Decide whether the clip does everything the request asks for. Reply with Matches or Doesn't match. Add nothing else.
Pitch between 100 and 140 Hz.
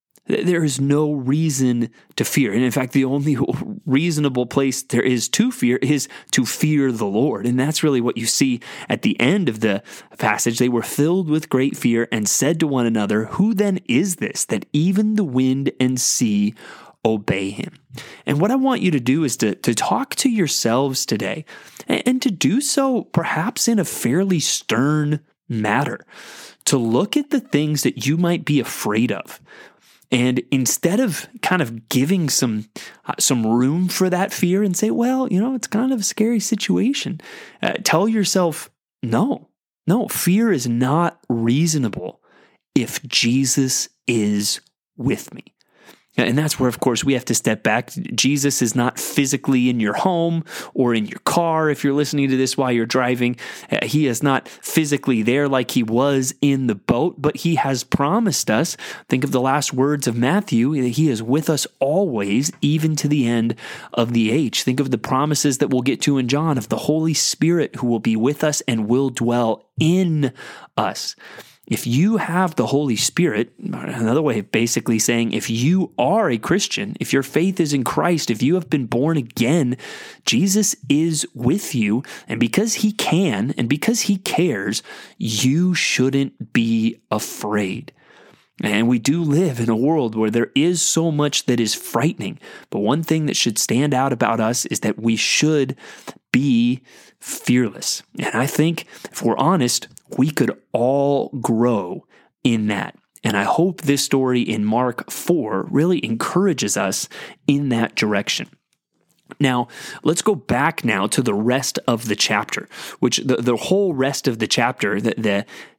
Matches